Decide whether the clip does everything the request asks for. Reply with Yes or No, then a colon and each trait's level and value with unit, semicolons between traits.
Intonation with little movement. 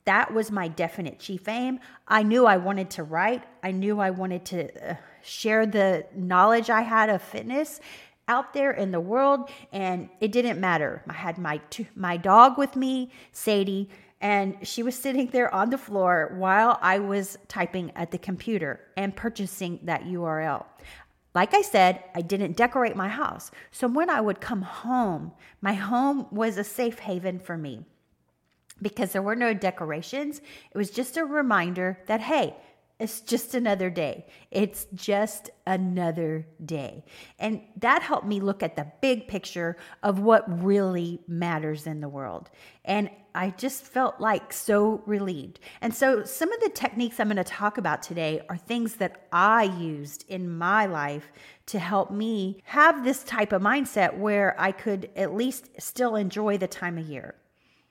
No: average, 4.4 semitones